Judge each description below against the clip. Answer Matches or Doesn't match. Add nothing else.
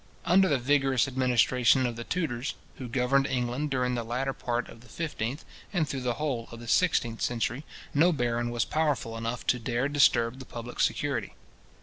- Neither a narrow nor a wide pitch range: Matches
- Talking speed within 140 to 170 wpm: Doesn't match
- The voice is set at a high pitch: Doesn't match